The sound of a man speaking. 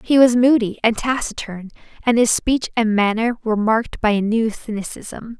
No: female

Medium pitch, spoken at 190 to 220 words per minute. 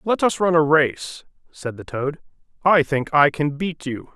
Yes: medium, 150 Hz; average, 200 wpm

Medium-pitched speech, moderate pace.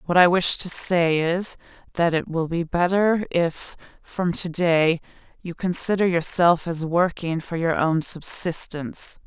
Yes: medium, 170 Hz; average, 155 wpm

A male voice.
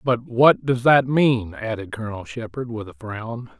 Yes: male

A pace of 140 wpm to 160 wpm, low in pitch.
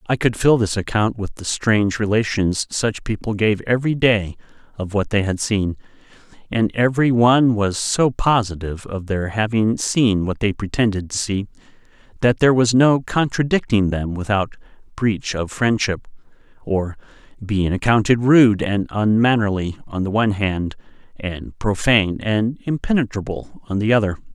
Yes: average, 150 wpm; low, 110 Hz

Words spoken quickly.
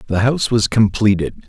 No: average, 160 wpm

